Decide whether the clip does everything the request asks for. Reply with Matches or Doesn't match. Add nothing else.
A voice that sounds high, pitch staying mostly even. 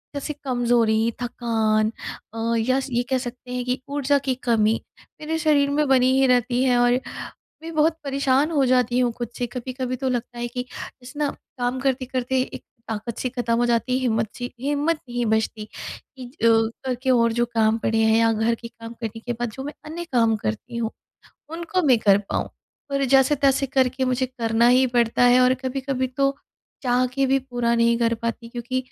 Matches